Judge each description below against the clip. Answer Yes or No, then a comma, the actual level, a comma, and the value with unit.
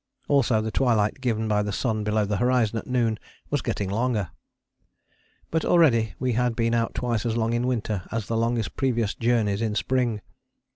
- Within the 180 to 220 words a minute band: Yes, average, 185 wpm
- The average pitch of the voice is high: No, low, 115 Hz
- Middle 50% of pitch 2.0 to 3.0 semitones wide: Yes, narrow, 2.4 semitones